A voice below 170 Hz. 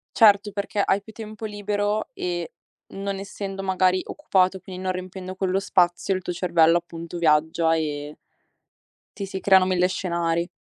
No: medium, 185 Hz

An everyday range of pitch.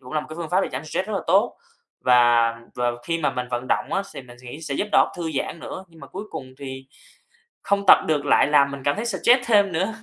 No: wide, 6.6 semitones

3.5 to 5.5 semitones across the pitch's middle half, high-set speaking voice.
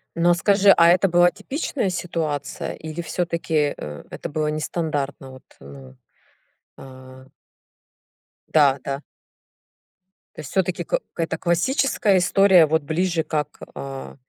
No: average, 3.8 semitones; medium, 160 Hz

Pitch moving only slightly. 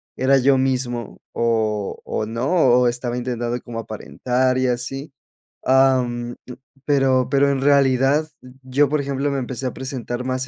Yes: narrow, 1.8 semitones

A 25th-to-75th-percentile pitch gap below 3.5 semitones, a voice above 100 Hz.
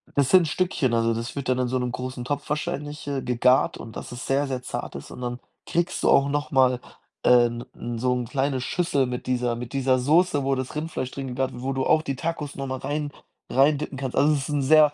Yes: narrow, 2.6 semitones; low, 135 Hz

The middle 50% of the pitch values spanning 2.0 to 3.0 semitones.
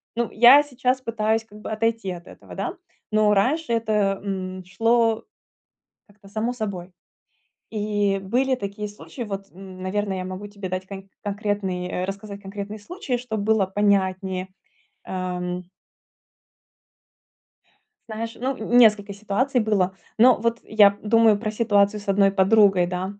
Yes: narrow, 2.6 semitones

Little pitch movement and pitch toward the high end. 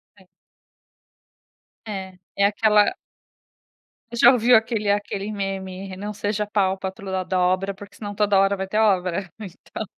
Yes: narrow, 1.7 semitones; high, 200 Hz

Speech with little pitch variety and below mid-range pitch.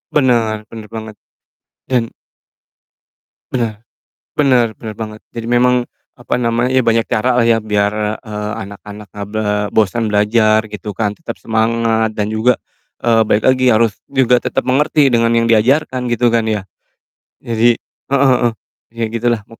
Yes: narrow, 2.1 semitones; low, 115 Hz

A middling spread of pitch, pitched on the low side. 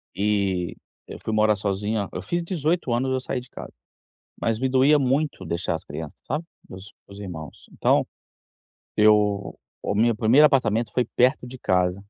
Yes: average, 4.7 semitones; low, 110 Hz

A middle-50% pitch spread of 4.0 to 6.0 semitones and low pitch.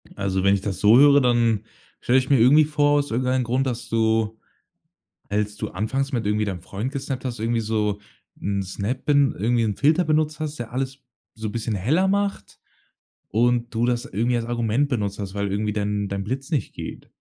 Yes: average, 4.3 semitones; low, 115 Hz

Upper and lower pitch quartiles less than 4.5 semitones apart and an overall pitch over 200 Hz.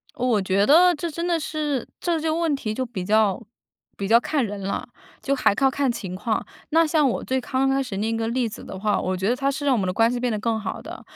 No: average, 5.3 semitones; high, 245 Hz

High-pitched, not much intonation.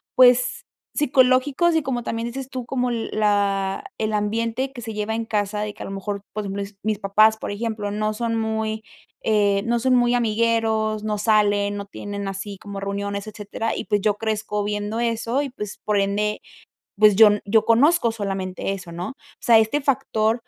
Yes: high, 215 Hz; narrow, 2.3 semitones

